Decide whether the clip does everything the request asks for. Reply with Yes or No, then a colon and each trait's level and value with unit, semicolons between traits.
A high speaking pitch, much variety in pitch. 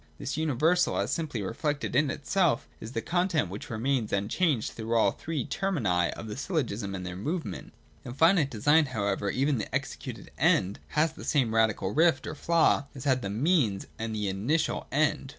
No: low, 130 Hz; wide, 6.5 semitones